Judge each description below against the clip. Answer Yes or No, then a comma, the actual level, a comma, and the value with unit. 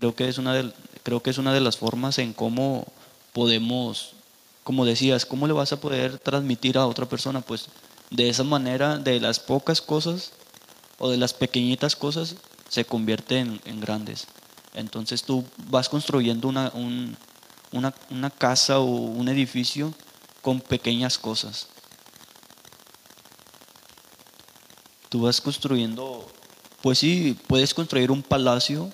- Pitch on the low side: Yes, low, 130 Hz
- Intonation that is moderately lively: No, narrow, 2.0 semitones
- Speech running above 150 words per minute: No, average, 140 wpm